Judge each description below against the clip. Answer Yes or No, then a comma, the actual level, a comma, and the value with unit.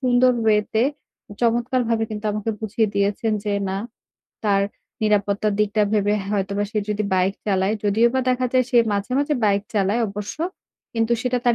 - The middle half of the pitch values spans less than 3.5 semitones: Yes, average, 2.8 semitones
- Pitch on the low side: No, high, 215 Hz